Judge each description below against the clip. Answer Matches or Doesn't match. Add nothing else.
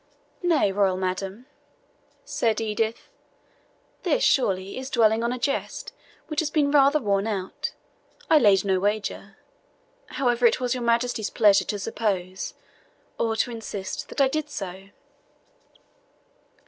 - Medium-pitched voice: Doesn't match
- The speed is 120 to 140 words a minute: Matches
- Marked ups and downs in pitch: Doesn't match